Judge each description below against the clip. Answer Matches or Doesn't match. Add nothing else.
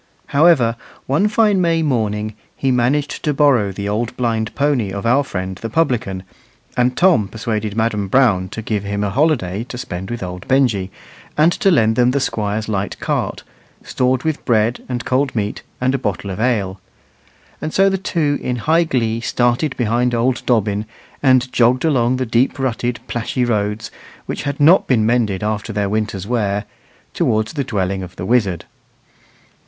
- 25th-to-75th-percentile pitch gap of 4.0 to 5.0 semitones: Matches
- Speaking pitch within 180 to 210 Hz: Doesn't match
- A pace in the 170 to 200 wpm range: Matches